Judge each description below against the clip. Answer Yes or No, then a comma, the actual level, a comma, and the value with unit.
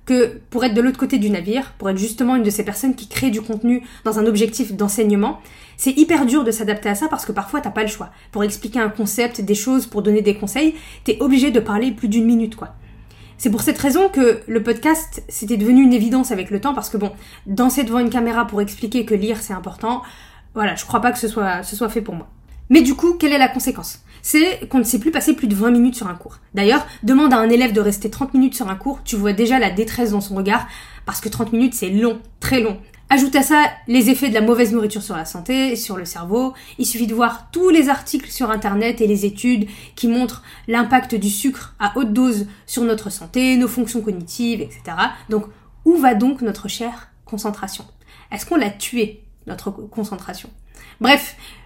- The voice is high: Yes, high, 230 Hz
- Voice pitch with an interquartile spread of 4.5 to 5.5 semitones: No, average, 3.5 semitones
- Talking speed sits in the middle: No, fast, 230 wpm